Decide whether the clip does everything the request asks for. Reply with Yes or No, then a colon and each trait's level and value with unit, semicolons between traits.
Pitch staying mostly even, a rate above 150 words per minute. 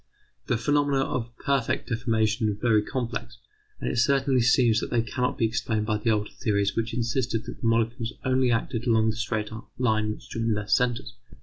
Yes: narrow, 2.1 semitones; average, 190 wpm